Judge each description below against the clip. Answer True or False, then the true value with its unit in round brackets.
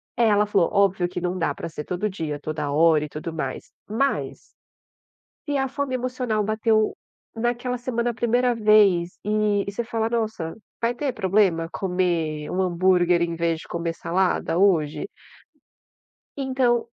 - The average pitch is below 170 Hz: False (200 Hz)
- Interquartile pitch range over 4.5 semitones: True (5.6 semitones)